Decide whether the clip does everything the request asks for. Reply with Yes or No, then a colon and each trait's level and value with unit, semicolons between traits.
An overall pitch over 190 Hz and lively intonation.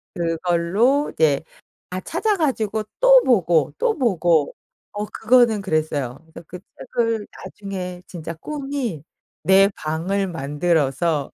No: medium, 185 Hz; wide, 6.2 semitones